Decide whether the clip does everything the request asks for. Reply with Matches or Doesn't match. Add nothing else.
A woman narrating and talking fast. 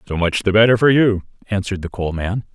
Doesn't match